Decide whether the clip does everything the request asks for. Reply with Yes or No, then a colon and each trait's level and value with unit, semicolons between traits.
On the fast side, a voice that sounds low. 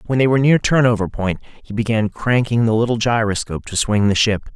Yes: fast, 210 wpm; low, 115 Hz